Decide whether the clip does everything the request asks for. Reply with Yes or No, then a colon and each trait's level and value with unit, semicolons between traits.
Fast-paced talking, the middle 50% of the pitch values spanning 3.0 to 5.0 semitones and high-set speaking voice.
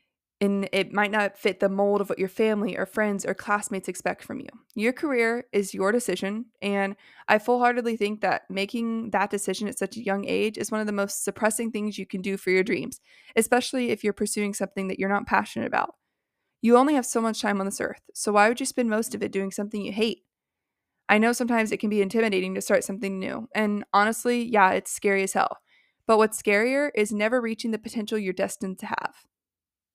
No: fast, 220 wpm; narrow, 2.4 semitones; high, 210 Hz